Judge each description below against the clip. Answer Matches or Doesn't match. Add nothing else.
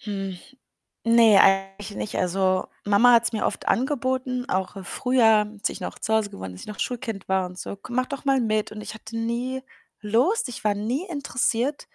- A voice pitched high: Matches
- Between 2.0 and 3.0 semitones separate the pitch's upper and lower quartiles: Doesn't match